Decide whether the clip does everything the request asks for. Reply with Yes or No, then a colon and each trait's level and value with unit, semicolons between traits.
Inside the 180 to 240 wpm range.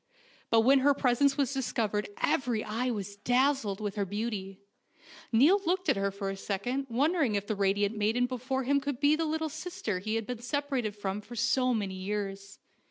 Yes: average, 195 wpm